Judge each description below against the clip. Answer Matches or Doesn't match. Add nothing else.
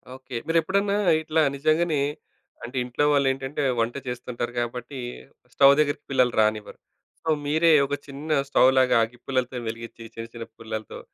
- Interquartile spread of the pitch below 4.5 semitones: Matches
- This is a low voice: Matches